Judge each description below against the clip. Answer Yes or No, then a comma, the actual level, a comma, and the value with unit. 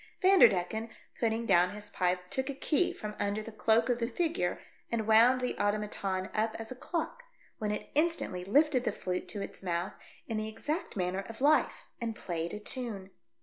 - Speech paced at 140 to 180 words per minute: No, average, 190 wpm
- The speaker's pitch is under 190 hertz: No, high, 220 Hz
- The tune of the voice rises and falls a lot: No, average, 4.3 semitones